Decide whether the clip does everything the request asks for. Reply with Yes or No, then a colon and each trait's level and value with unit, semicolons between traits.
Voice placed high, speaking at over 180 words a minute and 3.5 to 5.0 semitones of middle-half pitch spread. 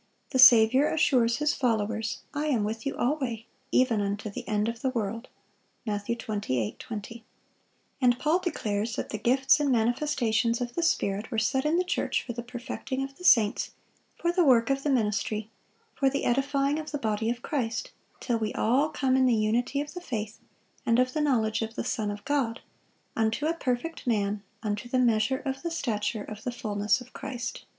Yes: high, 240 Hz; average, 190 wpm; average, 3.9 semitones